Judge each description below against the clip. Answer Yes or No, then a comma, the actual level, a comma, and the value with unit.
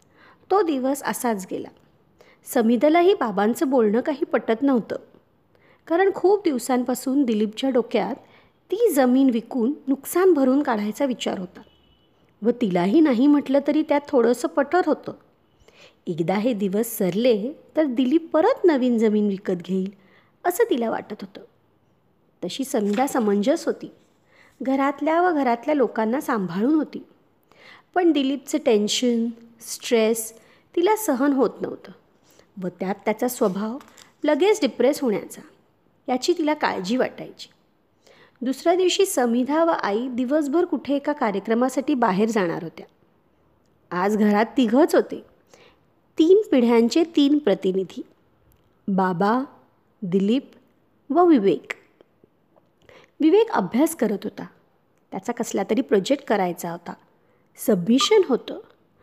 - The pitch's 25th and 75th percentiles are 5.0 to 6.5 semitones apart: Yes, wide, 5.6 semitones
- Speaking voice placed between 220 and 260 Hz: Yes, very high, 255 Hz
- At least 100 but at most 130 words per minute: Yes, average, 115 wpm